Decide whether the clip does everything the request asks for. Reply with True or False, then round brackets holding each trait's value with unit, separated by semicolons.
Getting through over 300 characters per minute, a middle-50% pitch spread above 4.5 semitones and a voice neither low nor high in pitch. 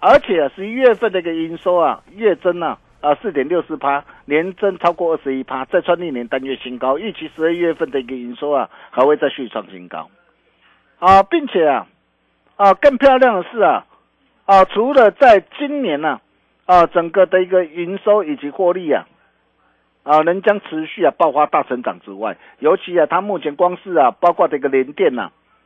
False (290 characters per minute; 5.2 semitones; 170 Hz)